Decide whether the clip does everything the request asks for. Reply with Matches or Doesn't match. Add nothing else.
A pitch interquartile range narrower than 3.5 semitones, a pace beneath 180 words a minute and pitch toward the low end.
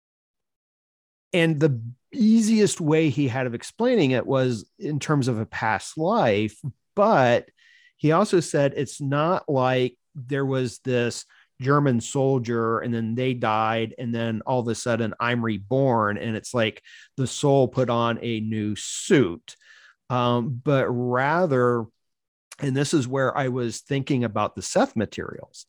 Doesn't match